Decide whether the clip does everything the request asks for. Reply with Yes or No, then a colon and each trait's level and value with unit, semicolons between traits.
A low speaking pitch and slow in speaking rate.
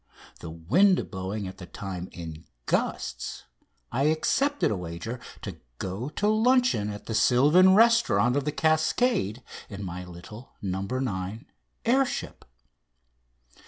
Yes: low, 115 Hz; slow, 130 wpm